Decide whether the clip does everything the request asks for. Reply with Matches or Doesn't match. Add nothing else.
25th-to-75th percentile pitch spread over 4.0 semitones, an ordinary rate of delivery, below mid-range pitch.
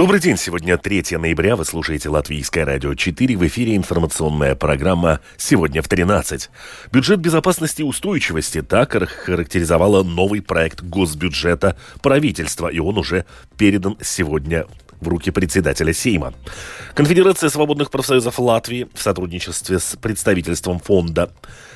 Matches